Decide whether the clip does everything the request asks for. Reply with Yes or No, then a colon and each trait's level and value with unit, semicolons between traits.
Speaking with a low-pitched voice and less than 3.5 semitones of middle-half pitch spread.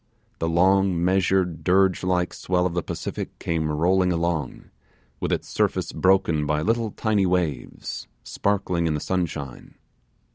Yes: very low, 90 Hz; narrow, 2.6 semitones